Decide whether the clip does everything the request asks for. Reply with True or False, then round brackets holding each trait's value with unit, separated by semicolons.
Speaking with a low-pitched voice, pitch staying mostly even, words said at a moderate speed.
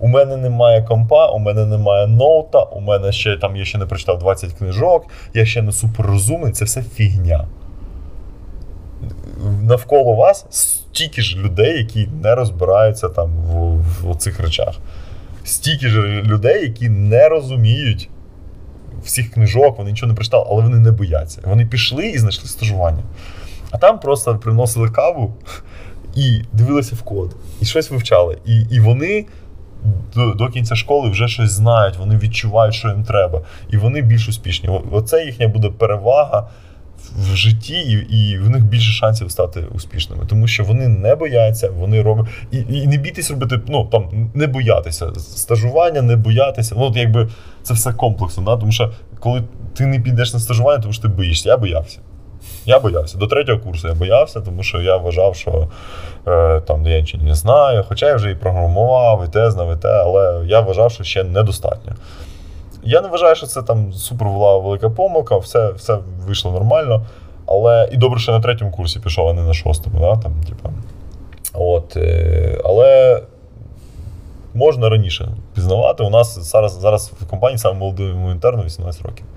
False (105 Hz; 4.0 semitones; 165 wpm)